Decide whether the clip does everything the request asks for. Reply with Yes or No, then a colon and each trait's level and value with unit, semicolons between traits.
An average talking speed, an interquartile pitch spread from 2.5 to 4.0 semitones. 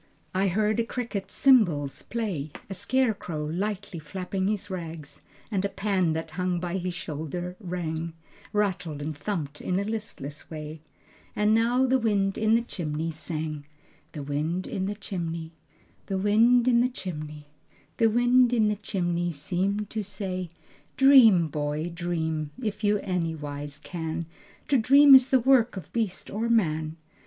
No: average, 155 wpm; average, 5.2 semitones